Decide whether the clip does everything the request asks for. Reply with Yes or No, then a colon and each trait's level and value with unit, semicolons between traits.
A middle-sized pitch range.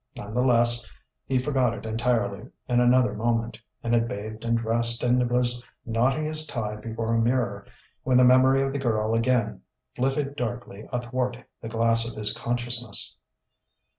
No: narrow, 1.7 semitones